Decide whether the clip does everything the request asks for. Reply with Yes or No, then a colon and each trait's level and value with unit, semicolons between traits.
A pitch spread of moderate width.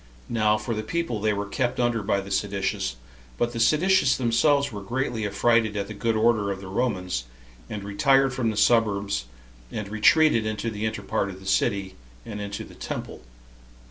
Yes: average, 3.0 semitones